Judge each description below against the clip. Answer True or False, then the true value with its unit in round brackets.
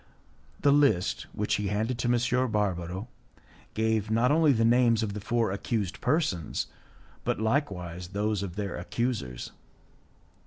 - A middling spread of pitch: True (3.7 semitones)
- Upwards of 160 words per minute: False (140 wpm)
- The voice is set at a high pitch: False (110 Hz)